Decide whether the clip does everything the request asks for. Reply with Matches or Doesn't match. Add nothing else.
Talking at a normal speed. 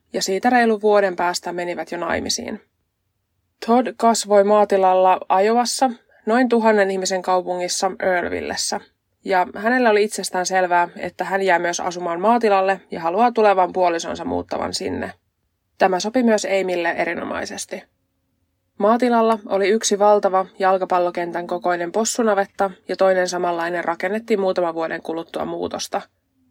Matches